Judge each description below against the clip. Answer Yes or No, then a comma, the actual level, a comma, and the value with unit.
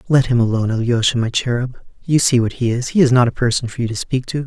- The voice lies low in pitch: Yes, low, 125 Hz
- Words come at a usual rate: No, fast, 280 wpm